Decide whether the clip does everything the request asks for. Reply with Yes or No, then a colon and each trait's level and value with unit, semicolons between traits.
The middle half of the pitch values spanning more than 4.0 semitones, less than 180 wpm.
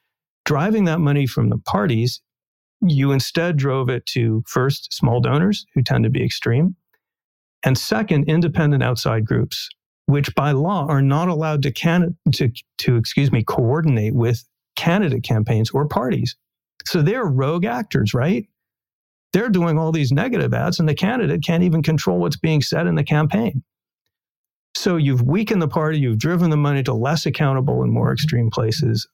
Yes: average, 5.0 semitones; average, 165 wpm